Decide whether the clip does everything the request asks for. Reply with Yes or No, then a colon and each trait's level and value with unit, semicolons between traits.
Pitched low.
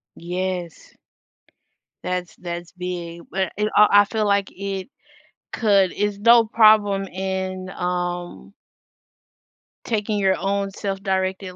No: high, 190 Hz